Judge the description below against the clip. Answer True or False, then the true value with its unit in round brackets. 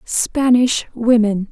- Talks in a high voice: True (230 Hz)